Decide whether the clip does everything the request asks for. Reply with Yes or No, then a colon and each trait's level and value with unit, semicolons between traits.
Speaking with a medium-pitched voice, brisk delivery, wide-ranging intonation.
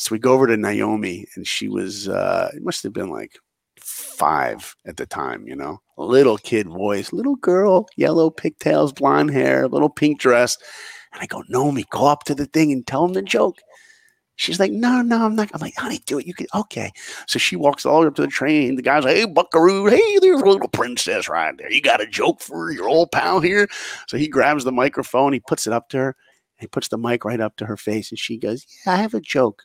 Yes: medium, 150 Hz; fast, 245 wpm; wide, 8.0 semitones